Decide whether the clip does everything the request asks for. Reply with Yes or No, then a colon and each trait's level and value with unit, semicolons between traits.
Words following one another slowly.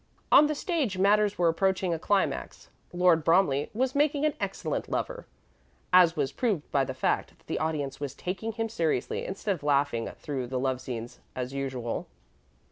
No: average, 175 wpm